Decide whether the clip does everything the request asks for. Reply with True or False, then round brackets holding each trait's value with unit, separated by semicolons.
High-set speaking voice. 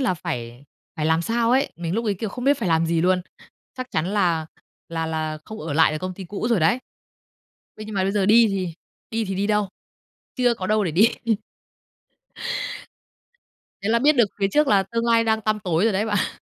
True (200 Hz)